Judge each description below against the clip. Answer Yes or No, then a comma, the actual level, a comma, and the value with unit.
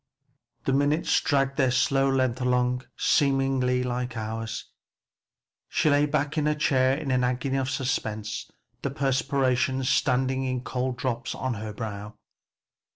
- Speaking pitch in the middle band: No, low, 130 Hz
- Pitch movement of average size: No, narrow, 1.7 semitones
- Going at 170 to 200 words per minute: No, average, 140 wpm